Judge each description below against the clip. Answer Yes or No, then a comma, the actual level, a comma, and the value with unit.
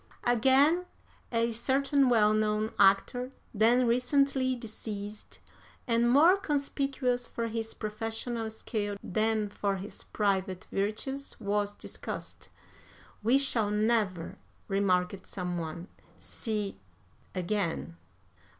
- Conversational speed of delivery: No, slow, 100 wpm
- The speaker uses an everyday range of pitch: Yes, average, 3.6 semitones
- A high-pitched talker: Yes, high, 220 Hz